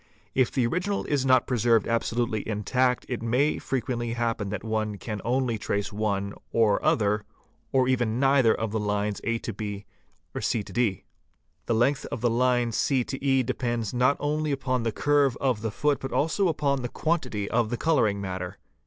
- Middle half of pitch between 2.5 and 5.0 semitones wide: Yes, average, 3.5 semitones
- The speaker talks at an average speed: Yes, average, 170 wpm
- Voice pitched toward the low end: Yes, low, 120 Hz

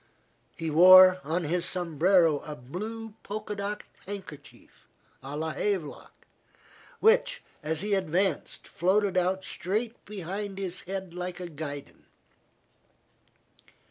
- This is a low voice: No, medium, 185 Hz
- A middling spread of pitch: Yes, average, 3.7 semitones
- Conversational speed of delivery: No, slow, 110 wpm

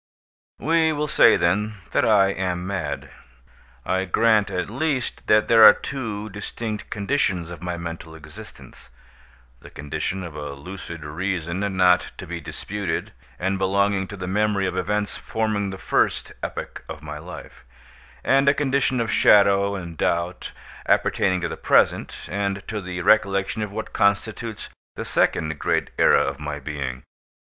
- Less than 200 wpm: Yes, average, 150 wpm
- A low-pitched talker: Yes, very low, 95 Hz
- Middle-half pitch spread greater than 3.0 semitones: Yes, average, 3.7 semitones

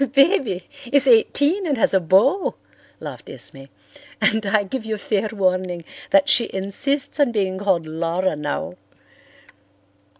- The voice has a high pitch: Yes, high, 205 Hz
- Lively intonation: Yes, wide, 6.7 semitones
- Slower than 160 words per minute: Yes, slow, 135 wpm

